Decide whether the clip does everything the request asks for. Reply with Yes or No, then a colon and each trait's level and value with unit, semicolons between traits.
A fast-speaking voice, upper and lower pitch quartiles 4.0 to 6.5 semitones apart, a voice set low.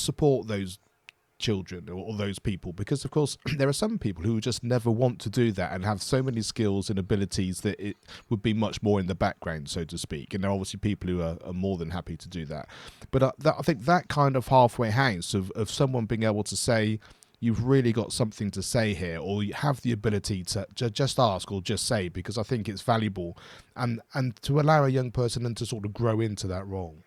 Yes: fast, 240 wpm; average, 4.5 semitones; low, 110 Hz